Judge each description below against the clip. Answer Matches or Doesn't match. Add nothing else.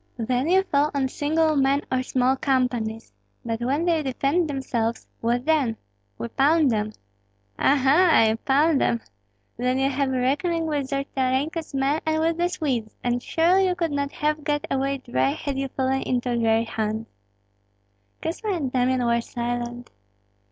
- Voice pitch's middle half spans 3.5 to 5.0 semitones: Matches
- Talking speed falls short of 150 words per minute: Doesn't match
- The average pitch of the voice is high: Matches